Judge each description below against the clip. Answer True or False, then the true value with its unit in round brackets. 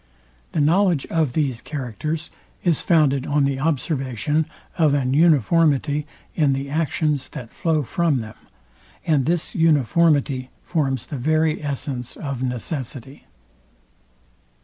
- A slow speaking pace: True (120 wpm)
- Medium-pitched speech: True (145 Hz)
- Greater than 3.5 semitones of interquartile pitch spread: False (3.1 semitones)